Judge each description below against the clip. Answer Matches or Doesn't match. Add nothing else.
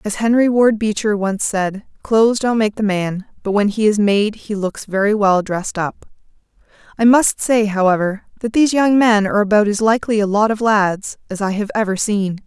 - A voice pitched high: Matches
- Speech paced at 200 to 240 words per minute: Matches